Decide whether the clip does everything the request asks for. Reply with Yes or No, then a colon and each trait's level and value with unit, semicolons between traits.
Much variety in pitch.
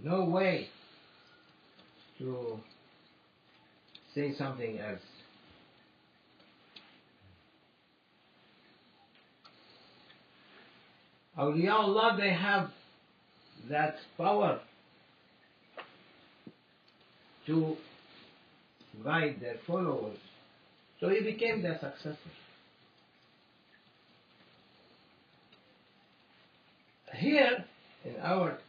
Yes: wide, 6.4 semitones